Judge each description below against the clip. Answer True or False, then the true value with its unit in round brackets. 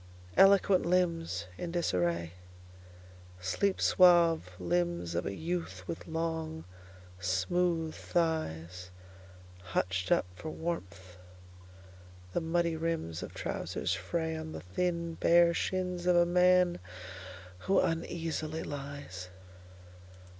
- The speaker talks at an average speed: False (90 wpm)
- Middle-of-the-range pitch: True (160 Hz)